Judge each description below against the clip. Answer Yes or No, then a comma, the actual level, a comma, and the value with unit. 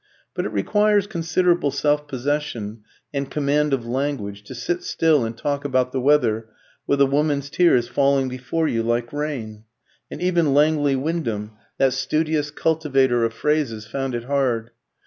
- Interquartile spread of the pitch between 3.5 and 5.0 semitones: Yes, average, 3.9 semitones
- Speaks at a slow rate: No, average, 155 wpm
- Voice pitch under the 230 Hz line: Yes, medium, 140 Hz